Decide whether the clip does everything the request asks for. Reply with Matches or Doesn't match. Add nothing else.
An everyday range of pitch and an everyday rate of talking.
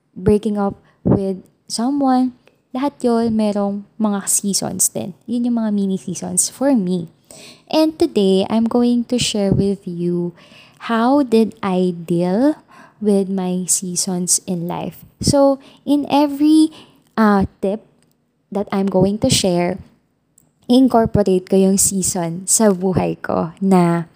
Matches